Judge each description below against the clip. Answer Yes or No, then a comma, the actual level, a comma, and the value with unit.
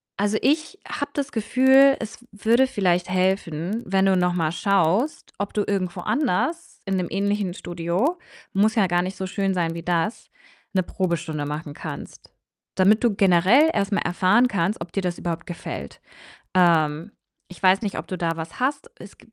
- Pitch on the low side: No, high, 190 Hz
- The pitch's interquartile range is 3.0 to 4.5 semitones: Yes, average, 4.0 semitones